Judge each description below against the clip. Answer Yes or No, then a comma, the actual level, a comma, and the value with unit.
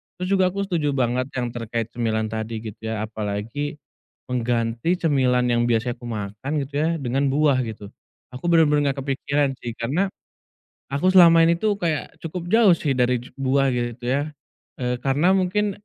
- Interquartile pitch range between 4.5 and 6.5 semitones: Yes, wide, 5.5 semitones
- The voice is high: No, low, 135 Hz